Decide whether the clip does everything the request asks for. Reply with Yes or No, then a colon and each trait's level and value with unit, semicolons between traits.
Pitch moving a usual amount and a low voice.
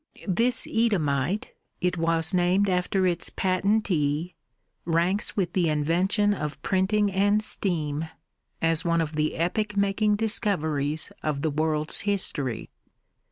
No: average, 4.4 semitones; medium, 180 Hz